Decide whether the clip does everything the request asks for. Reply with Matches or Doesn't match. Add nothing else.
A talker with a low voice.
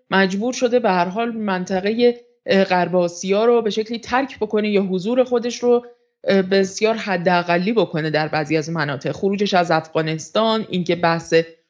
Doesn't match